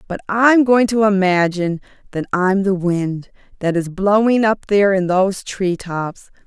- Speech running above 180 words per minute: No, average, 165 wpm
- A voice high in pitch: Yes, high, 195 Hz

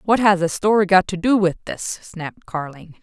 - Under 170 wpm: No, fast, 220 wpm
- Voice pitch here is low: No, medium, 185 Hz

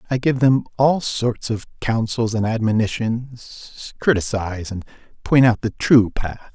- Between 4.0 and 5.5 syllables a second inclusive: Yes, 4.2 syllables/s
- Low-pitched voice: Yes, low, 115 Hz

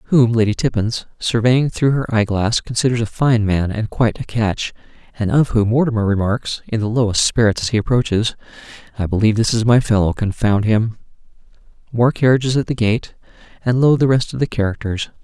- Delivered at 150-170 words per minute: No, average, 190 wpm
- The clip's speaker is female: No, male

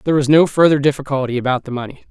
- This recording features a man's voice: Yes, male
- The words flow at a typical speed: No, fast, 230 wpm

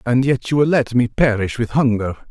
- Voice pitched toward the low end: Yes, low, 120 Hz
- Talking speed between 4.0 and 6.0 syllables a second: Yes, 5.3 syllables/s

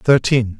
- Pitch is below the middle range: Yes, low, 120 Hz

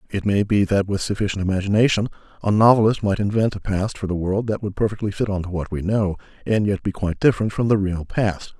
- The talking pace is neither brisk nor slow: No, fast, 235 wpm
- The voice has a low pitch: Yes, low, 100 Hz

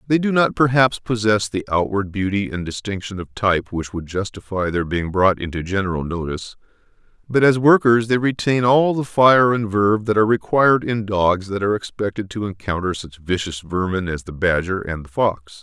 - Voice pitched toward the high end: No, low, 100 Hz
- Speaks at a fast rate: No, average, 190 wpm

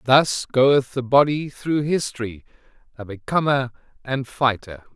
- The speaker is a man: Yes, male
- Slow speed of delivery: Yes, slow, 120 wpm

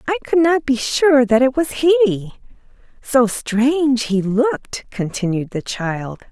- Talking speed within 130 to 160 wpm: Yes, average, 140 wpm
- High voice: Yes, very high, 255 Hz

